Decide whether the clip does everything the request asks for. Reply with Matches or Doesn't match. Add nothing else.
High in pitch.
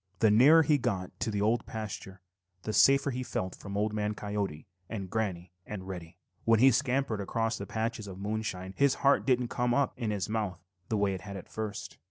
Doesn't match